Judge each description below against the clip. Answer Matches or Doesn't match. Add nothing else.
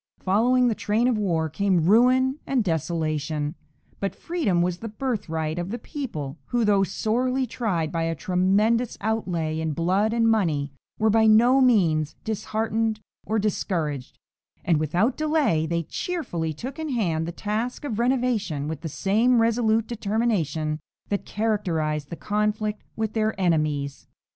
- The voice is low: Doesn't match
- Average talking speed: Matches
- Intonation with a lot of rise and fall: Matches